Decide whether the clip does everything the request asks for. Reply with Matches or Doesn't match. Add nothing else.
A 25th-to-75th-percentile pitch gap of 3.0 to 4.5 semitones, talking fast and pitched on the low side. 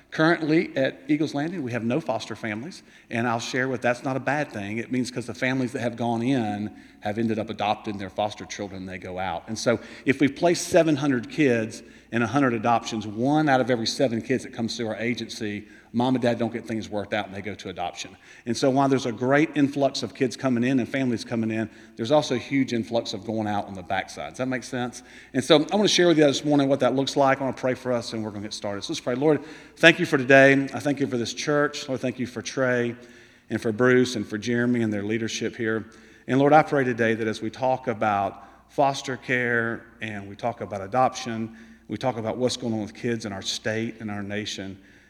Matches